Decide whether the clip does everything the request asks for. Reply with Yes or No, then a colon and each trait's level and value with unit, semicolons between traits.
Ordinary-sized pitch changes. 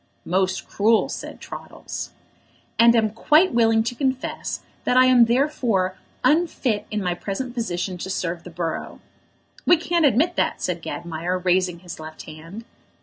No: wide, 6.1 semitones